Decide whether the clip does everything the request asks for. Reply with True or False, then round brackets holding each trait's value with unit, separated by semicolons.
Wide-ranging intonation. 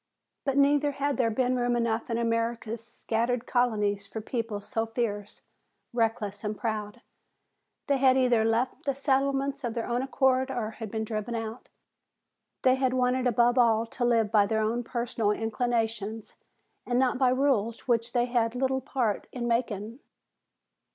False (2.4 semitones)